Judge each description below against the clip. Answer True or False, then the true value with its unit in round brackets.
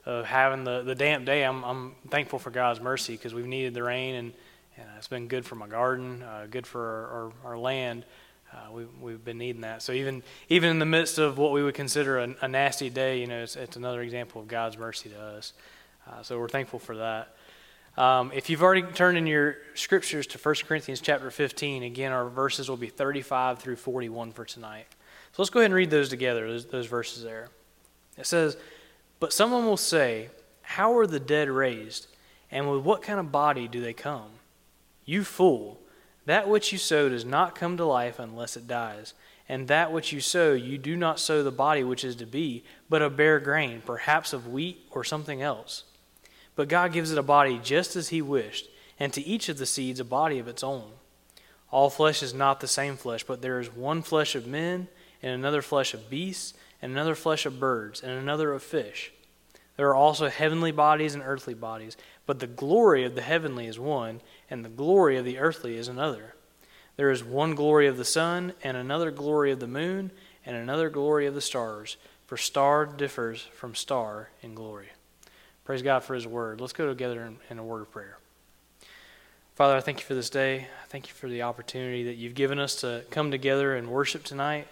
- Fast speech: True (215 wpm)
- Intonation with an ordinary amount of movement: True (3.7 semitones)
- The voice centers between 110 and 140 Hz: True (135 Hz)